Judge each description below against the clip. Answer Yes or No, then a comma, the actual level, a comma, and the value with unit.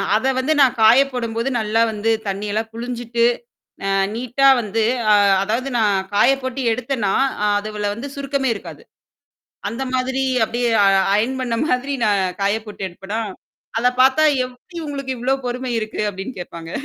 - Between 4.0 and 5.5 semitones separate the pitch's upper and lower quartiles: No, average, 3.6 semitones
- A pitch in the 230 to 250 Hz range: Yes, high, 235 Hz